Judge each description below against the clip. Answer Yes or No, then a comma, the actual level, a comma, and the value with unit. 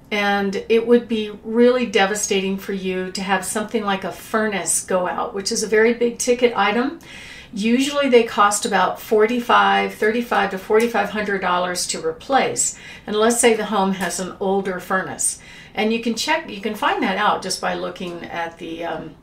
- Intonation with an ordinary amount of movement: Yes, average, 3.5 semitones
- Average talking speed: Yes, average, 180 wpm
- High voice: Yes, high, 210 Hz